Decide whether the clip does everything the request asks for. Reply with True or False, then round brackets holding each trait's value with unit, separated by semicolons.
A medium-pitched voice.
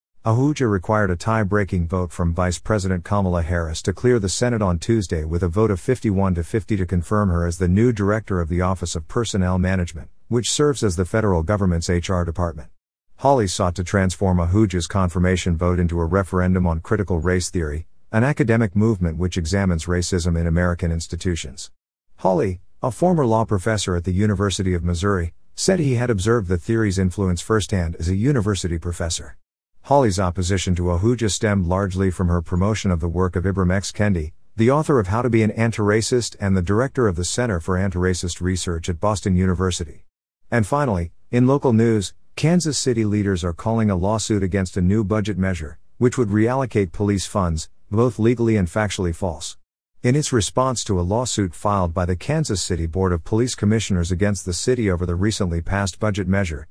False (95 Hz)